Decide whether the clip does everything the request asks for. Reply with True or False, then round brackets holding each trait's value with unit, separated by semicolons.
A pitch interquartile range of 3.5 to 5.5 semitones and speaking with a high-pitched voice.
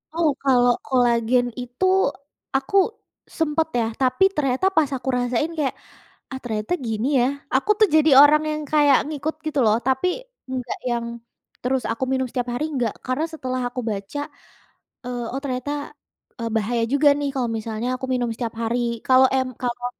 False (3.0 semitones; 255 Hz)